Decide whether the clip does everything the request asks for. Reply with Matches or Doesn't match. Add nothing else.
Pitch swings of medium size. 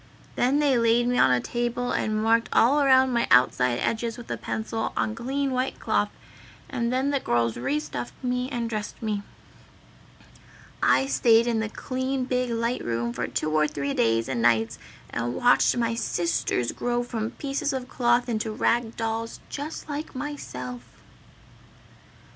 Doesn't match